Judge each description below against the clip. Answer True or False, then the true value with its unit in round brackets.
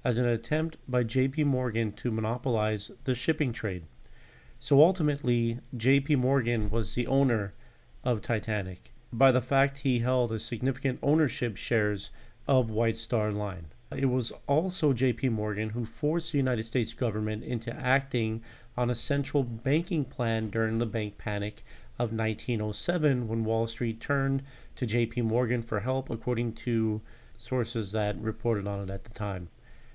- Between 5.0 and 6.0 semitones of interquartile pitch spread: False (3.0 semitones)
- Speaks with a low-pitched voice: True (120 Hz)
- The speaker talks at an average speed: True (150 wpm)